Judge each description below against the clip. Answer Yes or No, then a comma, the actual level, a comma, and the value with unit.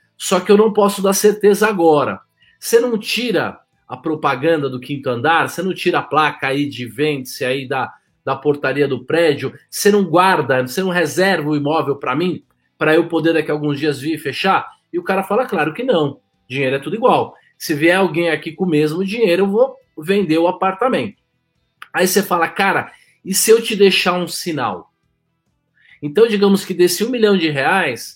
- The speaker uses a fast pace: Yes, fast, 195 wpm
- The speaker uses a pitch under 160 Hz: No, medium, 175 Hz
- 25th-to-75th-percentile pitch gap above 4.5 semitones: Yes, average, 5.1 semitones